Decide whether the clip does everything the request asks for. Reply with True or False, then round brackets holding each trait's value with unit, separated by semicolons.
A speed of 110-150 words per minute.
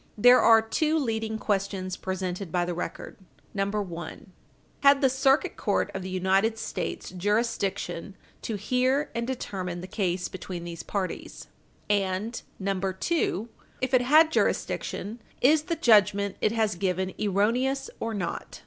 True (140 wpm)